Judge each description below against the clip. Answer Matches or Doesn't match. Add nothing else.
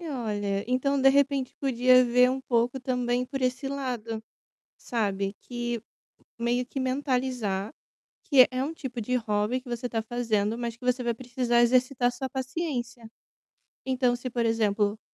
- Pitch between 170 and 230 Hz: Doesn't match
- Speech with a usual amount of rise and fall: Doesn't match